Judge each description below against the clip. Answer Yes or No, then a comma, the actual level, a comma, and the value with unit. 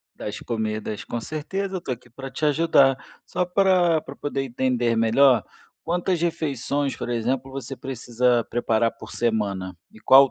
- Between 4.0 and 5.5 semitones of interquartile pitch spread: Yes, average, 4.5 semitones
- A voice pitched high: No, low, 130 Hz